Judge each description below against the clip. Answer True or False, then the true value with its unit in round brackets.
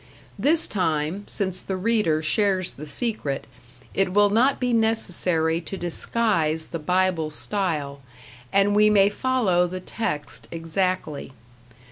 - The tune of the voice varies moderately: True (4.5 semitones)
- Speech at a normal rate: False (125 wpm)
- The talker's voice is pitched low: False (185 Hz)